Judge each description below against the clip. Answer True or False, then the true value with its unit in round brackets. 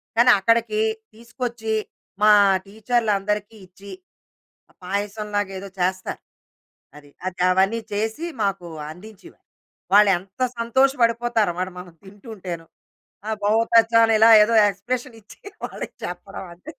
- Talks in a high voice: True (210 Hz)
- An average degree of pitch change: True (3.0 semitones)